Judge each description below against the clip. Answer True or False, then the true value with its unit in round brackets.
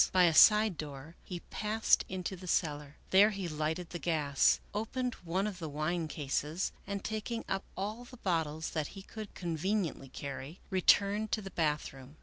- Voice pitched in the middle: True (175 Hz)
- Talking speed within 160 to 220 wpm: True (170 wpm)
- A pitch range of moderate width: True (4.8 semitones)